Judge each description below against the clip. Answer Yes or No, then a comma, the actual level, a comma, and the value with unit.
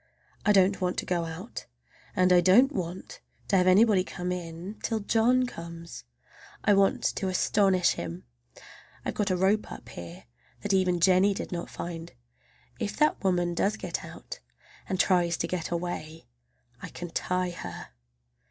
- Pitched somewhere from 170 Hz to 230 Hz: Yes, medium, 185 Hz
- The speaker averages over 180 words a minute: No, average, 160 wpm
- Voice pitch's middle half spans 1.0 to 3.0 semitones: Yes, narrow, 2.5 semitones